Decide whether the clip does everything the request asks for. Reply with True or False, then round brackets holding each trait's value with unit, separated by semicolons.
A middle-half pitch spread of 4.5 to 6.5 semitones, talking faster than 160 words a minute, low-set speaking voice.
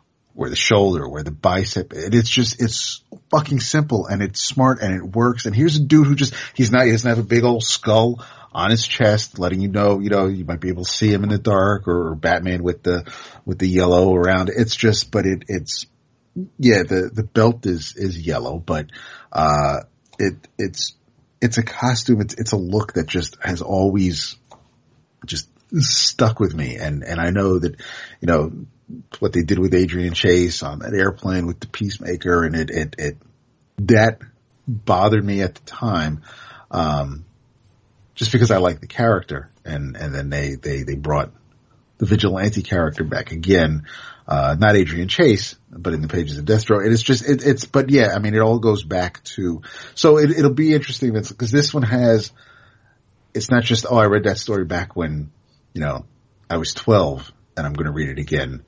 True (5.1 semitones; 190 wpm; 105 Hz)